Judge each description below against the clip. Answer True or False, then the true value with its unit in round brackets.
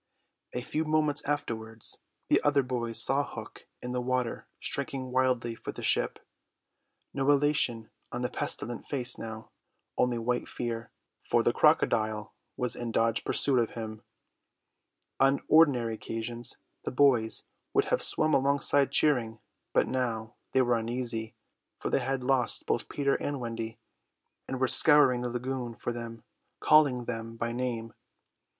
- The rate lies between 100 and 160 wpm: True (145 wpm)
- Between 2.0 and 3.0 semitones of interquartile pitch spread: True (2.7 semitones)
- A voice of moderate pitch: False (125 Hz)